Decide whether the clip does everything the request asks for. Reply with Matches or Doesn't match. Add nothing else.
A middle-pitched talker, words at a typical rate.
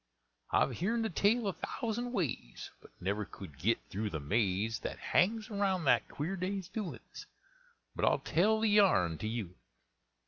Matches